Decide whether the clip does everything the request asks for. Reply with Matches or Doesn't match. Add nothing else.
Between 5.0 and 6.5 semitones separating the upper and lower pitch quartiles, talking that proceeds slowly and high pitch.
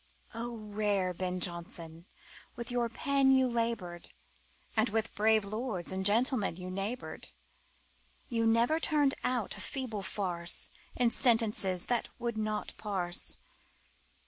Doesn't match